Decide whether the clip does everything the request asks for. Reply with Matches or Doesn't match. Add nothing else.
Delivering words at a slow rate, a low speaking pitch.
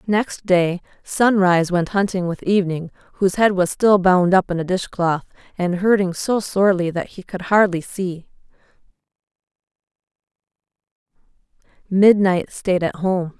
Doesn't match